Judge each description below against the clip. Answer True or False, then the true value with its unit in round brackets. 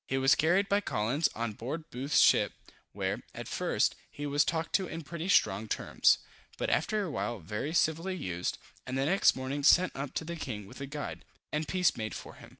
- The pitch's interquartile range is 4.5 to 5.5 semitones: True (4.9 semitones)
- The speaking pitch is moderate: True (145 Hz)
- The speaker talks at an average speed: False (210 wpm)